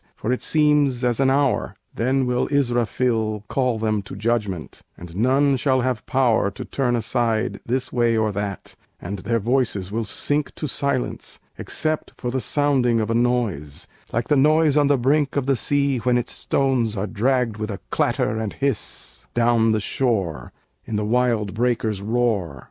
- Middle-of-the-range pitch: No, low, 120 Hz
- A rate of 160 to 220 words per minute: Yes, average, 175 wpm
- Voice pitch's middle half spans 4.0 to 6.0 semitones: No, average, 3.6 semitones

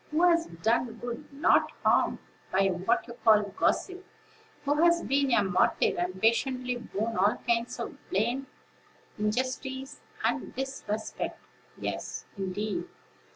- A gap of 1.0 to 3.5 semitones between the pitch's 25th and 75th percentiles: No, average, 4.4 semitones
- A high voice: Yes, high, 235 Hz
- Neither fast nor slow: No, slow, 125 wpm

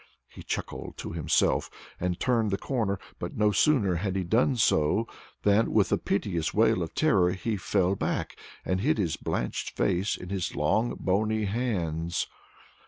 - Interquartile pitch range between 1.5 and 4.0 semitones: Yes, average, 3.7 semitones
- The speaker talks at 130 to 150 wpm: No, average, 165 wpm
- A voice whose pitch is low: Yes, low, 100 Hz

